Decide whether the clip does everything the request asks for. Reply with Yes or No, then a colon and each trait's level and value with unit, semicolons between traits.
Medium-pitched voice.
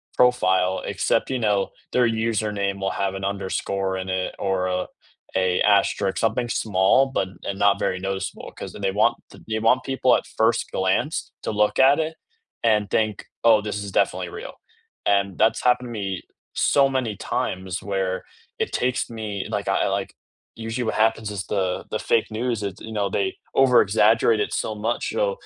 No: low, 105 Hz